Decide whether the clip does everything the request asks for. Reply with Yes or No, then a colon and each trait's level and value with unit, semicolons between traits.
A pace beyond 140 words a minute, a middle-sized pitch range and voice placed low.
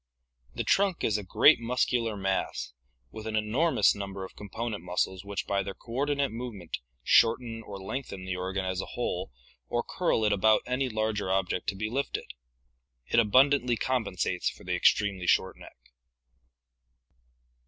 Yes: average, 155 wpm; average, 4.0 semitones; low, 110 Hz